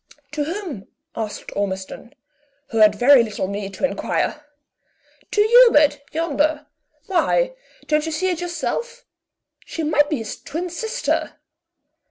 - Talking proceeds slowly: Yes, slow, 130 wpm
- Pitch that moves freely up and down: Yes, wide, 7.5 semitones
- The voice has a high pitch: Yes, very high, 300 Hz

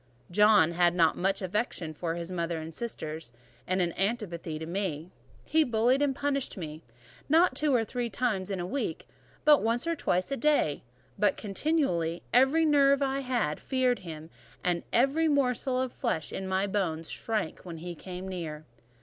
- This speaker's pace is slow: No, average, 175 wpm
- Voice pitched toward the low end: No, high, 195 Hz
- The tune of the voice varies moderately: No, wide, 7.4 semitones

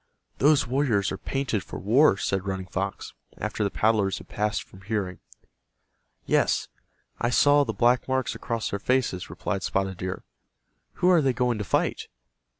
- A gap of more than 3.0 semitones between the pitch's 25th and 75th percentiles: Yes, average, 5.2 semitones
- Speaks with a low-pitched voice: Yes, low, 110 Hz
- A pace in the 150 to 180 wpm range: Yes, average, 160 wpm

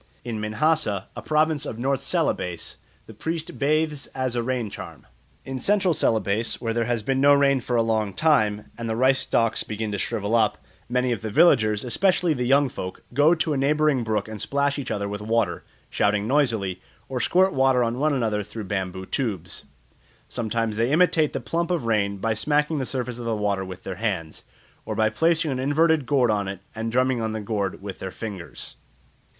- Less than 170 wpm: No, average, 200 wpm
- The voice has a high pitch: No, low, 115 Hz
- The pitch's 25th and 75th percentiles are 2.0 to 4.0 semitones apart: No, average, 5.1 semitones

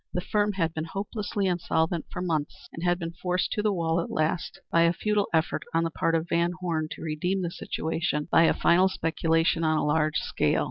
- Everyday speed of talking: No, fast, 220 wpm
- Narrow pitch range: Yes, narrow, 2.0 semitones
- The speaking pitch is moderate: Yes, medium, 170 Hz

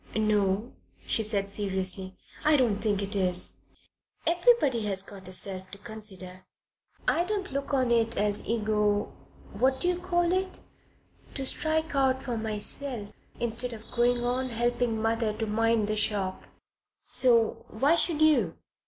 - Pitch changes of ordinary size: Yes, average, 4.4 semitones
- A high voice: Yes, high, 225 Hz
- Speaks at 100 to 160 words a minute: Yes, average, 150 wpm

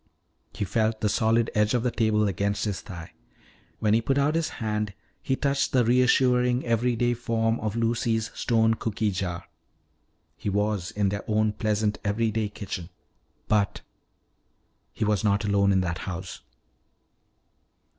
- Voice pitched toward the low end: Yes, low, 110 Hz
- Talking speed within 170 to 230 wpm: No, average, 145 wpm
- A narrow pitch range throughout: Yes, narrow, 2.3 semitones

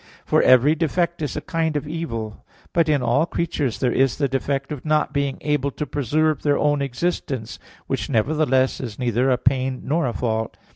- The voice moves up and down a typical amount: Yes, average, 3.3 semitones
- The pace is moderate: Yes, average, 190 wpm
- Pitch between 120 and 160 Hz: Yes, medium, 140 Hz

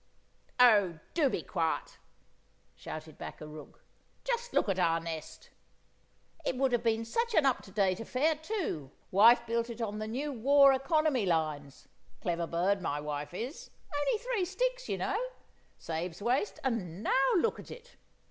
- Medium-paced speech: Yes, average, 155 wpm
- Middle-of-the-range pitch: No, high, 230 Hz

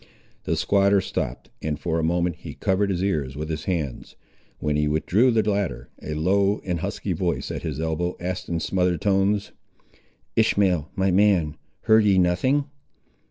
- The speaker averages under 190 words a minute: Yes, average, 165 wpm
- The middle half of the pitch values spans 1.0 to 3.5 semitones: No, average, 3.9 semitones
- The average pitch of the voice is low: Yes, very low, 90 Hz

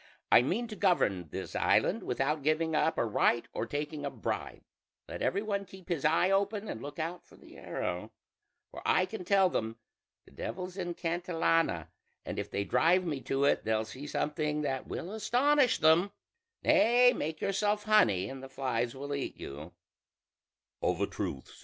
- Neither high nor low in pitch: Yes, medium, 160 Hz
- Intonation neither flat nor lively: No, wide, 6.4 semitones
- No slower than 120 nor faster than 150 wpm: No, average, 170 wpm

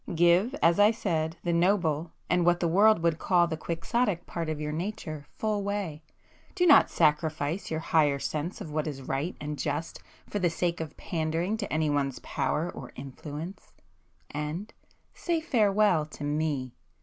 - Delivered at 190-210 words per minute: No, average, 155 wpm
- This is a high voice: No, medium, 165 Hz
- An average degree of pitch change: Yes, average, 3.9 semitones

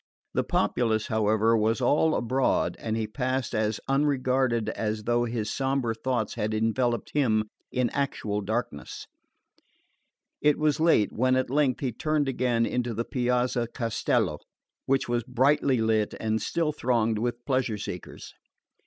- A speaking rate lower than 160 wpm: Yes, average, 145 wpm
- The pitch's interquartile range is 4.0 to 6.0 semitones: No, average, 3.0 semitones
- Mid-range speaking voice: No, low, 120 Hz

